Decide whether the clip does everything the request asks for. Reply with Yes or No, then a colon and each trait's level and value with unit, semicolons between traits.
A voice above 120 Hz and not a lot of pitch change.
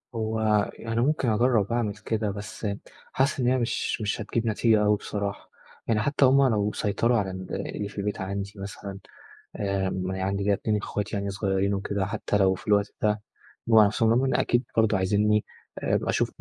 No: low, 105 Hz; narrow, 2.2 semitones